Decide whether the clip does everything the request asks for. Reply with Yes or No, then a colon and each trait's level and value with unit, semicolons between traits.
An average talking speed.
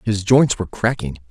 Yes: average, 185 wpm